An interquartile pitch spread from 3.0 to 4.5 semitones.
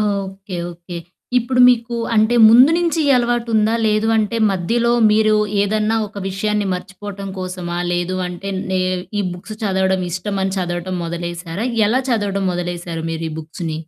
Yes: average, 3.6 semitones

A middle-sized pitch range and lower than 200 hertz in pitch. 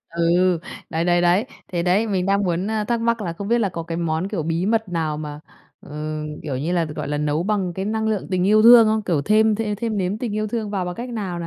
Yes: average, 4.3 semitones; medium, 185 Hz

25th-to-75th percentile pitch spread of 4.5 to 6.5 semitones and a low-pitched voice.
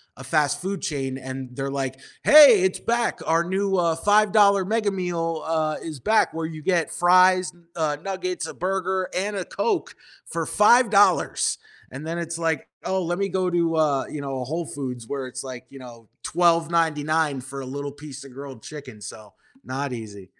No: average, 5.3 semitones; medium, 160 Hz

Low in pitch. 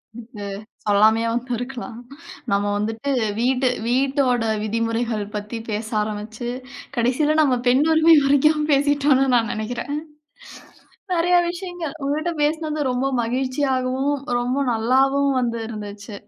No: very high, 255 Hz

